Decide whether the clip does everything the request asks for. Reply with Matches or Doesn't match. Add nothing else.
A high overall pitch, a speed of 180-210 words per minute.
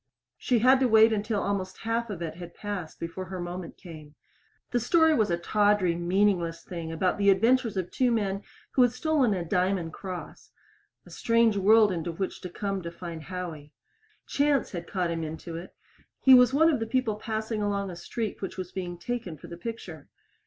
Matches